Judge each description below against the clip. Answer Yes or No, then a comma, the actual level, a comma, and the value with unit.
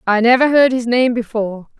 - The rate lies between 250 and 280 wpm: No, average, 200 wpm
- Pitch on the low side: No, high, 235 Hz